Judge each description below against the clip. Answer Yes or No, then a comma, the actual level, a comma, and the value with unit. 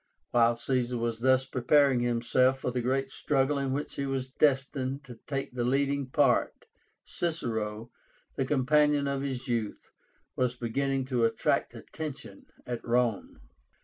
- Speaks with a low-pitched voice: Yes, low, 130 Hz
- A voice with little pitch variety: Yes, narrow, 2.3 semitones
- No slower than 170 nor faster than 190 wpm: No, average, 145 wpm